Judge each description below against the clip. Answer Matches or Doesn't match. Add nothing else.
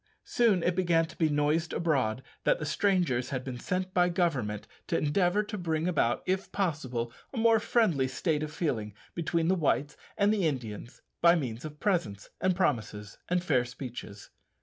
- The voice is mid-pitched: Matches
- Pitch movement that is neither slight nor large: Doesn't match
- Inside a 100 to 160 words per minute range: Doesn't match